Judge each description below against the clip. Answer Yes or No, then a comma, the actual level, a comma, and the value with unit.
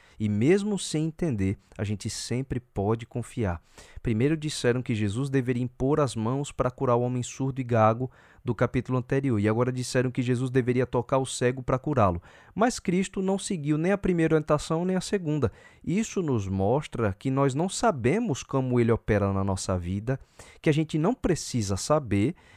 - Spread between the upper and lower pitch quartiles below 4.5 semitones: No, average, 5.3 semitones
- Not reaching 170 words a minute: No, average, 180 wpm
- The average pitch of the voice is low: Yes, low, 130 Hz